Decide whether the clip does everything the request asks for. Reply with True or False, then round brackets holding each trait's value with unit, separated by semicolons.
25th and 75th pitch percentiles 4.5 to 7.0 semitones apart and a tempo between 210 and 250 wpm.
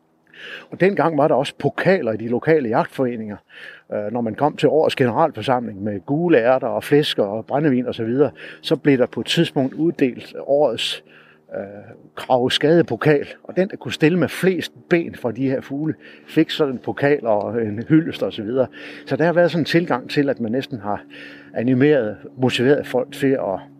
False (4.8 semitones; 190 wpm)